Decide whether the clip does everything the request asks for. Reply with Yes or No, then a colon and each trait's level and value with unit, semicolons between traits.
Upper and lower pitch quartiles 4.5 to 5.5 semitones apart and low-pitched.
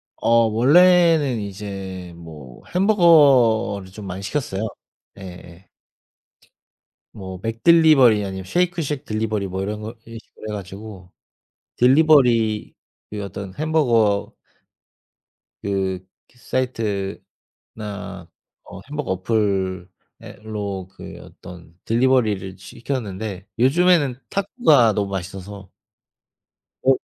Yes: average, 5.2 semitones; low, 105 Hz